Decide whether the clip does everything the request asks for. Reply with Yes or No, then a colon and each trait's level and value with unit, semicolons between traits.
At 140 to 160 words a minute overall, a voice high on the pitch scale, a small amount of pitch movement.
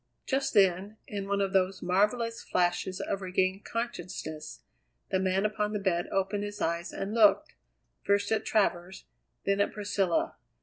Yes: average, 150 wpm; high, 195 Hz; narrow, 2.0 semitones